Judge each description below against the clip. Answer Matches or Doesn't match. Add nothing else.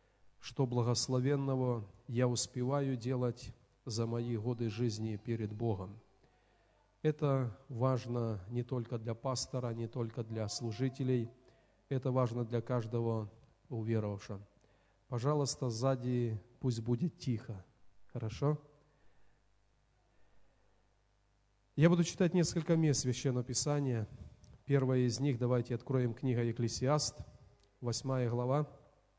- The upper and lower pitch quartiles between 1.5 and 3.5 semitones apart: Matches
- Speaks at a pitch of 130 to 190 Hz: Doesn't match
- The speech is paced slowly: Matches